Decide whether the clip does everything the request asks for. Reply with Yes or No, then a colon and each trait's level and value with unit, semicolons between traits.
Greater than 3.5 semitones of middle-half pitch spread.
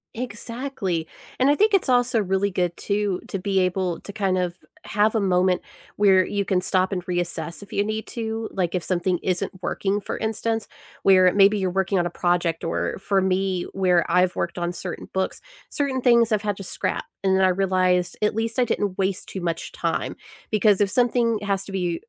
No: average, 2.7 semitones